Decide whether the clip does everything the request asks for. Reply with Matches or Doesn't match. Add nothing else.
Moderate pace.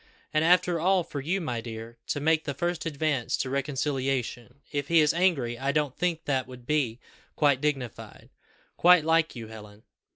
Matches